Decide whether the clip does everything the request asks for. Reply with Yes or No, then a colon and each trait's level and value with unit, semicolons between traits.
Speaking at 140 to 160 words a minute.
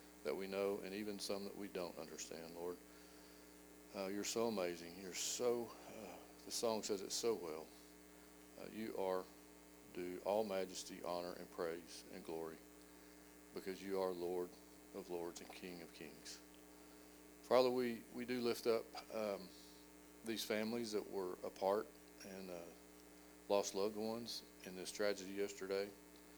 Yes: average, 150 wpm